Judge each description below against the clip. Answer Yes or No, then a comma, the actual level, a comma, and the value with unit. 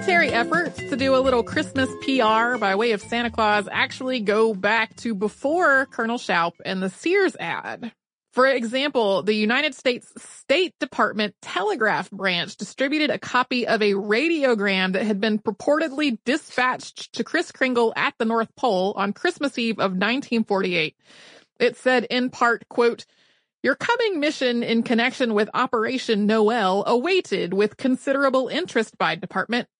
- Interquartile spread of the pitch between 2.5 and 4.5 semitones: Yes, average, 3.7 semitones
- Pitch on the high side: Yes, high, 235 Hz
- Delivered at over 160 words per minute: No, average, 150 wpm